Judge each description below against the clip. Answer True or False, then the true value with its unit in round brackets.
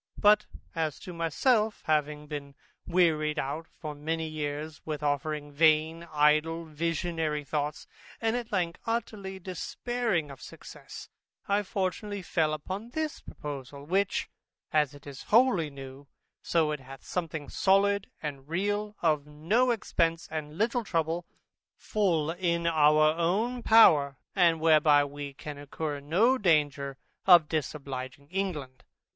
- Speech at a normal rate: False (130 wpm)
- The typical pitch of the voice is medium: True (160 Hz)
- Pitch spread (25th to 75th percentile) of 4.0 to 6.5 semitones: True (4.4 semitones)